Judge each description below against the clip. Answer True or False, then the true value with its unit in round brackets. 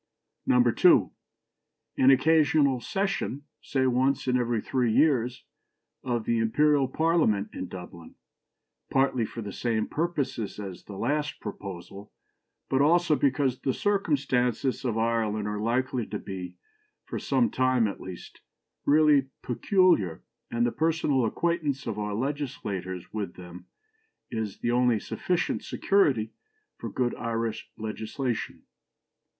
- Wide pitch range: False (4.7 semitones)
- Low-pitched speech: True (125 Hz)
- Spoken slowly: True (125 wpm)